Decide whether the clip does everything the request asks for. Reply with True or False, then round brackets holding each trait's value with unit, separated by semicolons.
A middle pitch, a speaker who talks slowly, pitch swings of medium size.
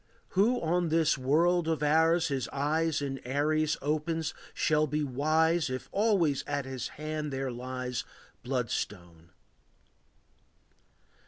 True (150 Hz; 120 wpm; 3.5 semitones)